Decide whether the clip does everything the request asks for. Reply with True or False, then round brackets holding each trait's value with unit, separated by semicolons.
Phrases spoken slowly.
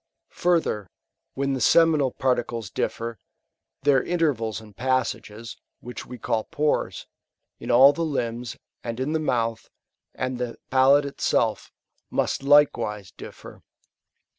True (120 wpm)